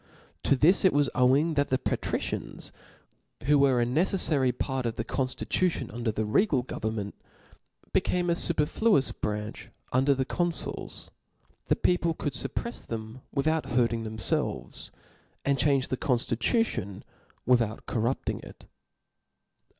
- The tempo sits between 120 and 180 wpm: Yes, average, 140 wpm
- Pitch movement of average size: Yes, average, 4.7 semitones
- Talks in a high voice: No, low, 130 Hz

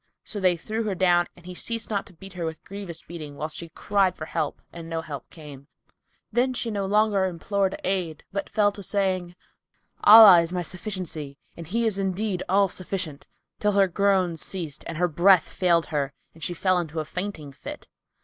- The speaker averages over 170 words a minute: Yes, average, 195 wpm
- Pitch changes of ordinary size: Yes, average, 3.3 semitones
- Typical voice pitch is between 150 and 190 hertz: Yes, medium, 185 Hz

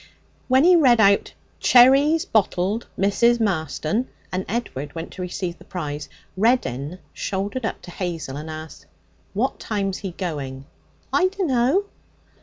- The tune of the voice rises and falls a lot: Yes, wide, 6.7 semitones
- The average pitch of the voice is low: No, high, 195 Hz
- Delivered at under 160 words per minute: Yes, slow, 135 wpm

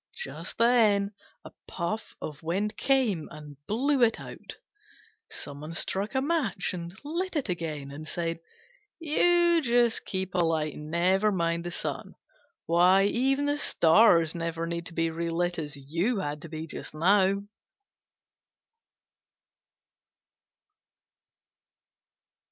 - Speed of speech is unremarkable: No, slow, 125 wpm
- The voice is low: No, medium, 180 Hz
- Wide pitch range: Yes, wide, 5.9 semitones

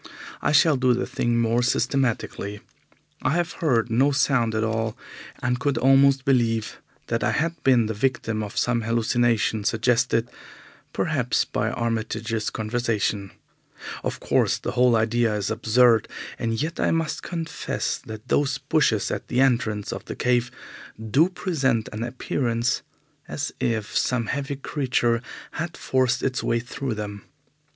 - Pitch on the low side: Yes, low, 120 Hz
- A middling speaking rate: Yes, average, 145 wpm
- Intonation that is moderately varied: Yes, average, 3.1 semitones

